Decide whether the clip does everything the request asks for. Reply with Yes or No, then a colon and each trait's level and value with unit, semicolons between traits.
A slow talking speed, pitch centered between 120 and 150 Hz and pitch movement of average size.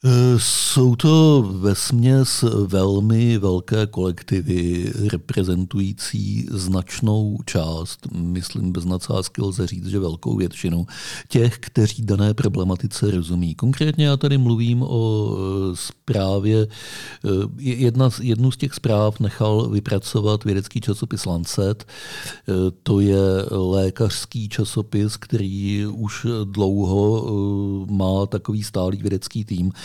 No: slow, 100 wpm; low, 105 Hz; average, 3.5 semitones